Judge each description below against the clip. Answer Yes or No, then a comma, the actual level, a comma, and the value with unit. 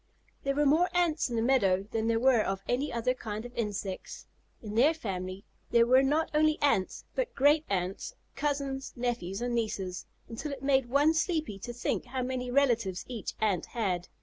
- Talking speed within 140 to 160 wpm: No, average, 185 wpm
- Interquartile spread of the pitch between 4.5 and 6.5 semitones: Yes, average, 5.1 semitones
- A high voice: Yes, high, 245 Hz